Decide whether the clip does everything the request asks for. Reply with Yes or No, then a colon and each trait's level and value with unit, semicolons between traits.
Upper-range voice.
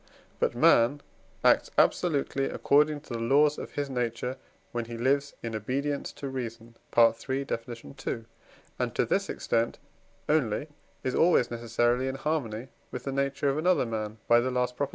No: low, 130 Hz